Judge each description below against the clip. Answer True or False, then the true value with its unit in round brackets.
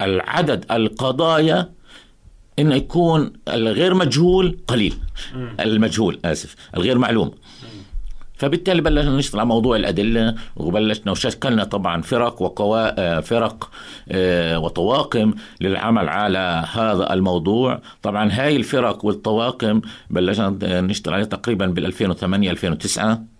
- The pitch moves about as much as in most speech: True (4.3 semitones)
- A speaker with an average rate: True (100 wpm)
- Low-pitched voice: True (110 Hz)